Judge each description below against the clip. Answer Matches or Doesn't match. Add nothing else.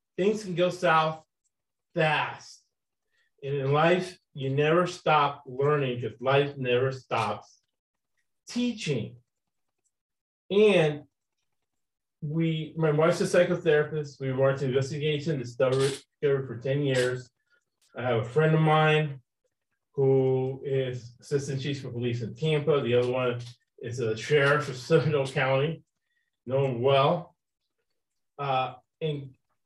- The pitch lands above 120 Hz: Matches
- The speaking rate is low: Matches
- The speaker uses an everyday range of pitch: Matches